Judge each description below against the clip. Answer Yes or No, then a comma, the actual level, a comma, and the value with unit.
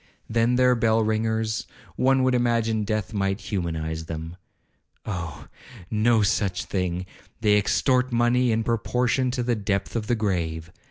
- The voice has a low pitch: Yes, low, 110 Hz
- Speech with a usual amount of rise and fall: Yes, average, 3.6 semitones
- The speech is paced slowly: Yes, slow, 130 wpm